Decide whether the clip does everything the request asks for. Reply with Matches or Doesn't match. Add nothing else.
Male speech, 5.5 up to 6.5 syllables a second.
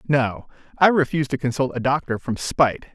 Matches